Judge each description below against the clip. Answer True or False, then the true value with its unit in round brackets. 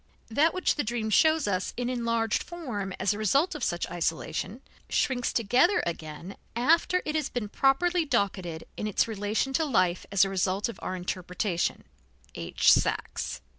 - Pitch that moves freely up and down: True (6.4 semitones)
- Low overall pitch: False (225 Hz)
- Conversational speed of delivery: True (165 wpm)